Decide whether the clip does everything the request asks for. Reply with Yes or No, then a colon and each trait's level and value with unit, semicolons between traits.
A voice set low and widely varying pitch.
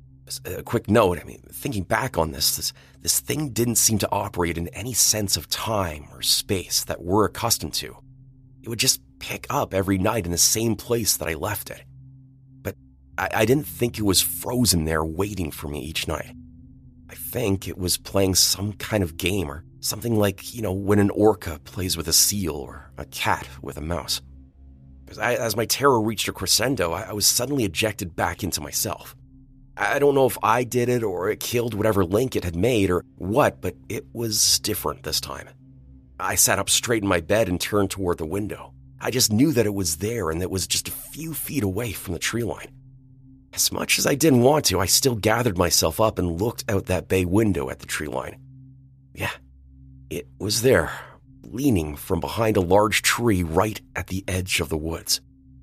Yes: low, 100 Hz; wide, 5.9 semitones